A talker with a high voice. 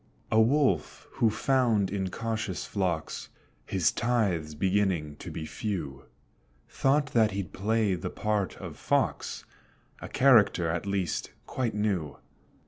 No: low, 100 Hz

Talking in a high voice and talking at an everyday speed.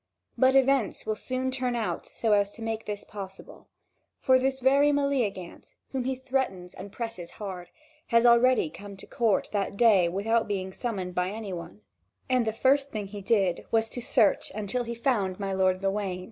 Yes: high, 220 Hz; average, 185 wpm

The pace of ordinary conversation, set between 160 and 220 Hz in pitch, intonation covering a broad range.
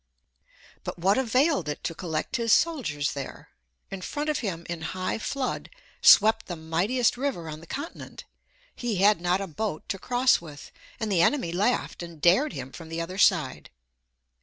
Yes: average, 175 wpm; high, 190 Hz; wide, 6.7 semitones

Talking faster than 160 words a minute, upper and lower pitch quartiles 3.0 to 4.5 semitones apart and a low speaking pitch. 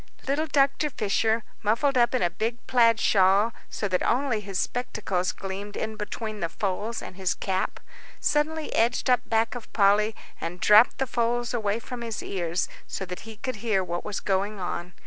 No: average, 185 wpm; average, 3.6 semitones; high, 215 Hz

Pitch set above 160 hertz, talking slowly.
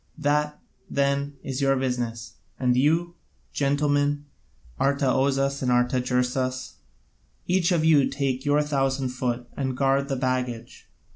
No: low, 135 Hz; slow, 120 wpm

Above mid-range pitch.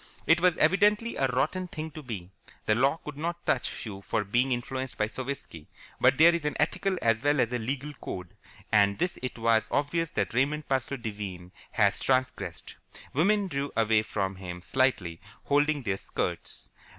No: low, 130 Hz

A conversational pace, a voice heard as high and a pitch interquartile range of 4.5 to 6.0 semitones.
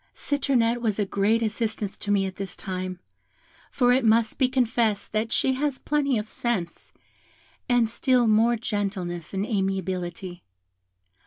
No: average, 145 wpm; high, 220 Hz; average, 3.8 semitones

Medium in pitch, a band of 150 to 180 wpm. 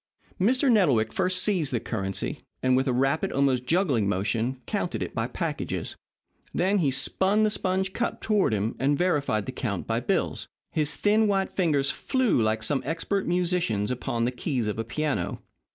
Yes: medium, 145 Hz; average, 175 wpm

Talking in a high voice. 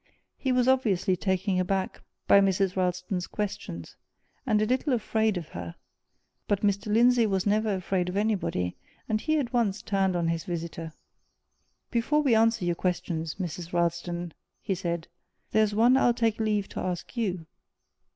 Yes: high, 195 Hz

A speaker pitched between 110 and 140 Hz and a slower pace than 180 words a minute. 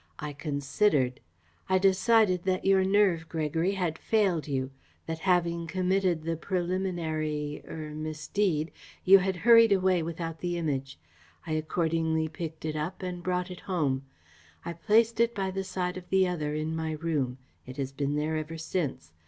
No: medium, 165 Hz; average, 160 wpm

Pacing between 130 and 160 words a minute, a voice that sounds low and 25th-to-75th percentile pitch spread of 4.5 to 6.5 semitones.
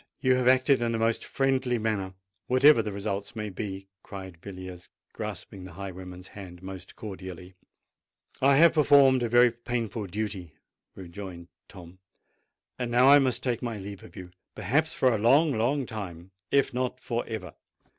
Yes: average, 155 wpm; low, 110 Hz; average, 5.1 semitones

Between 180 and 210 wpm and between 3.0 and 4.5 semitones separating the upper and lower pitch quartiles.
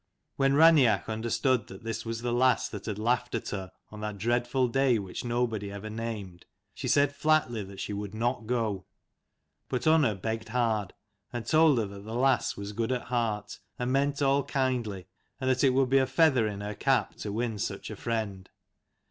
Yes: average, 195 wpm; average, 3.6 semitones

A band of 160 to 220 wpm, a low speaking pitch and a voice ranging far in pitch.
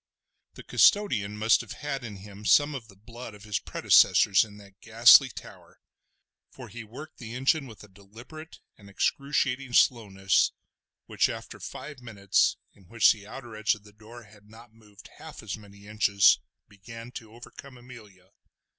No: average, 165 wpm; low, 110 Hz; average, 3.1 semitones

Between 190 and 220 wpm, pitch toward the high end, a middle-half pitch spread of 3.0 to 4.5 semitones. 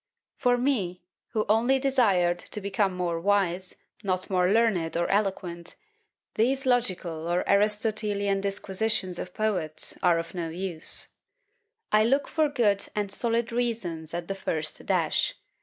No: average, 140 wpm; high, 200 Hz; average, 4.2 semitones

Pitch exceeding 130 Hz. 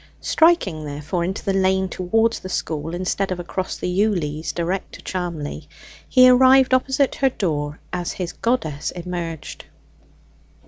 Yes: medium, 185 Hz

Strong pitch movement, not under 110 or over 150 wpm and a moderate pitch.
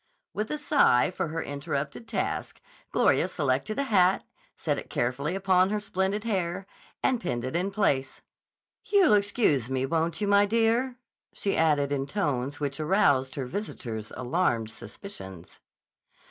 Yes: wide, 7.0 semitones; average, 145 wpm; medium, 175 Hz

